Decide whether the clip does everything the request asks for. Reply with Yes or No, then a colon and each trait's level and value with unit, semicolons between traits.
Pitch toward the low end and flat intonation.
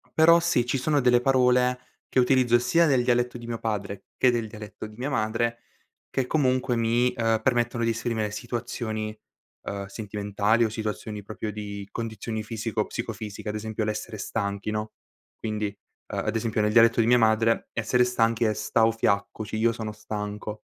Yes: low, 115 Hz; narrow, 2.2 semitones